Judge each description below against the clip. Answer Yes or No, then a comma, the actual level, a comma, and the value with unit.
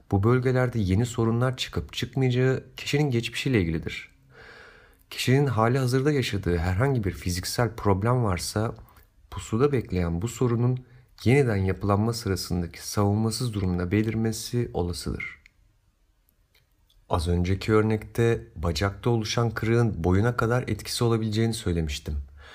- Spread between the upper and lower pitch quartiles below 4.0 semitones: No, average, 4.9 semitones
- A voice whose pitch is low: Yes, low, 110 Hz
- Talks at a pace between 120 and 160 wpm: No, average, 105 wpm